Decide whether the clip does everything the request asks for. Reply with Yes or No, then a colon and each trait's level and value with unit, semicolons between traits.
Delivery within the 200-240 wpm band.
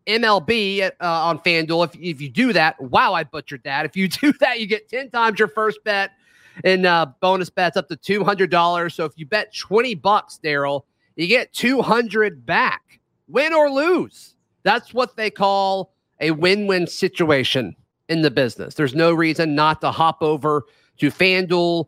No: average, 180 wpm